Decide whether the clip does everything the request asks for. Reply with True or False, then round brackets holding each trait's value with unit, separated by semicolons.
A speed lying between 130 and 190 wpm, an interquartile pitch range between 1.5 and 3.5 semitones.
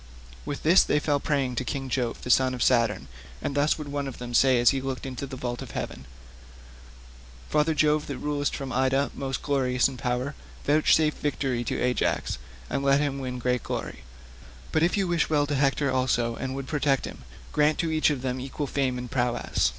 False (205 wpm; 2.6 semitones)